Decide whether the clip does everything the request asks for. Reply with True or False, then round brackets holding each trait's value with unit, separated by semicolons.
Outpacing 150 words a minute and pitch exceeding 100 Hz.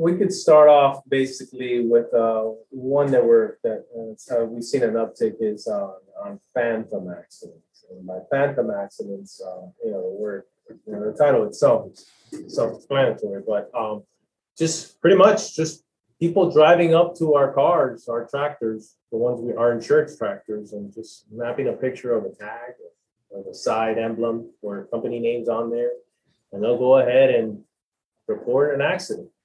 True (170 wpm; 135 Hz)